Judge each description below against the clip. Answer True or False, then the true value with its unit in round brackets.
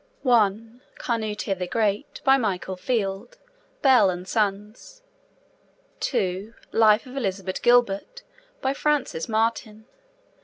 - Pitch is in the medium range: False (220 Hz)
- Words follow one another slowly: True (105 wpm)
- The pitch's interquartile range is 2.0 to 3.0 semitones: False (4.2 semitones)